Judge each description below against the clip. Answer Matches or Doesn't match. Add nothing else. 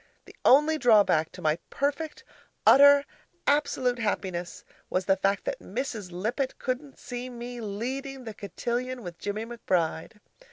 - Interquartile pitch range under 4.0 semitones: Doesn't match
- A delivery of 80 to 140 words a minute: Matches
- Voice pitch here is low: Doesn't match